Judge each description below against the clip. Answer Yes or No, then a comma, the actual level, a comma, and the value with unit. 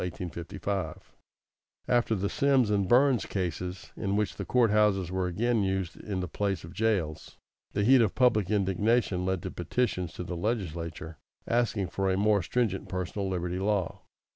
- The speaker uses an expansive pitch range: No, average, 3.4 semitones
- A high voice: No, very low, 95 Hz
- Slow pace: No, average, 160 wpm